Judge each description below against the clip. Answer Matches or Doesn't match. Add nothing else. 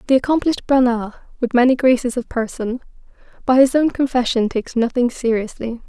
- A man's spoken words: Doesn't match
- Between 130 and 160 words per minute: Matches